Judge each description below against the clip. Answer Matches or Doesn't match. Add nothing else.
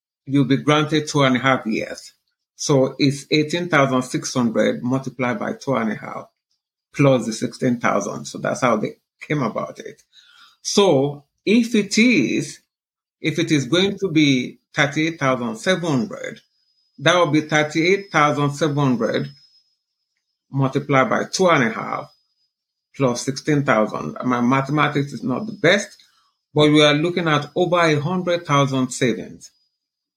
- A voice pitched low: Doesn't match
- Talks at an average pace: Doesn't match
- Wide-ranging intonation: Doesn't match